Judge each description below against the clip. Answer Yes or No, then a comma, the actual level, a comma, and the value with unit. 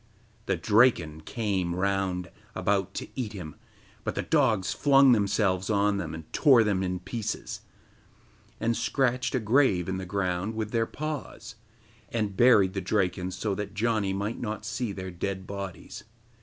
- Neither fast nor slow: Yes, average, 155 wpm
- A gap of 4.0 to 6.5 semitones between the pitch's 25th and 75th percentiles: No, average, 3.4 semitones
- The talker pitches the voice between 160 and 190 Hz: No, low, 100 Hz